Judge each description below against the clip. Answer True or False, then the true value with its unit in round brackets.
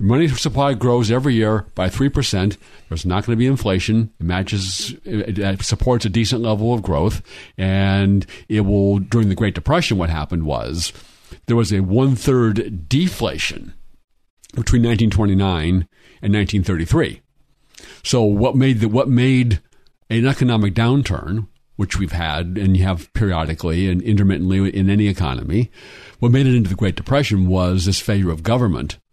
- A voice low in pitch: True (105 Hz)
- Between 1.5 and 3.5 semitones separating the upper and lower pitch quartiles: False (4.2 semitones)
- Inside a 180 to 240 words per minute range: False (155 wpm)